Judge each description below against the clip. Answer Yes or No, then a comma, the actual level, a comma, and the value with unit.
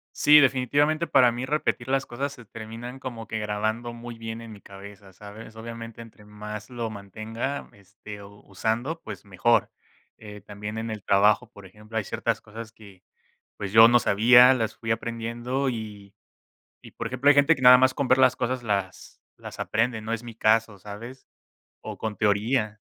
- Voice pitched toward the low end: Yes, low, 115 Hz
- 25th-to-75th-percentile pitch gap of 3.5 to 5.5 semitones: No, average, 2.8 semitones